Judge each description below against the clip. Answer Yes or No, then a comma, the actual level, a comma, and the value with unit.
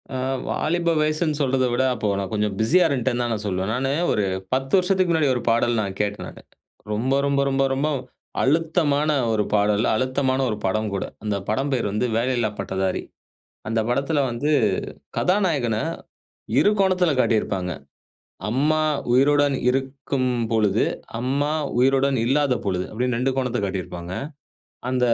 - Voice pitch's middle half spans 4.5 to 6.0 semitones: Yes, average, 4.9 semitones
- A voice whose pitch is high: No, low, 130 Hz